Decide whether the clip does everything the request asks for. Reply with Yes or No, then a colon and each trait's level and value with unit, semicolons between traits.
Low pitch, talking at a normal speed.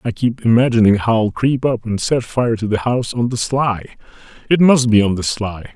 No: low, 115 Hz; fast, 230 wpm